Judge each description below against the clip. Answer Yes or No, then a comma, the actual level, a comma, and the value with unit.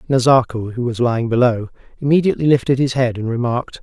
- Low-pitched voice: Yes, low, 125 Hz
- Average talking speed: Yes, average, 170 wpm